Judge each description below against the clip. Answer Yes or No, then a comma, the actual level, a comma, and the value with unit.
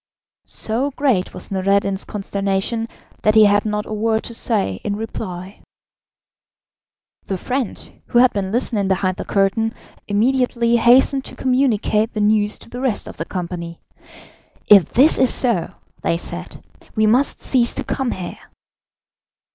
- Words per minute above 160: No, average, 145 wpm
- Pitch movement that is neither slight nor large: Yes, average, 3.4 semitones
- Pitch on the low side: No, high, 215 Hz